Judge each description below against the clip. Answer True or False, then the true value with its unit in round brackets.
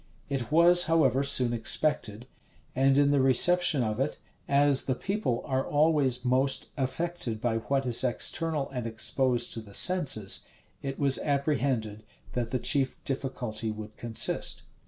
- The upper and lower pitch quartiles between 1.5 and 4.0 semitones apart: True (3.3 semitones)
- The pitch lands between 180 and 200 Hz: False (135 Hz)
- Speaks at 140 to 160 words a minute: True (150 wpm)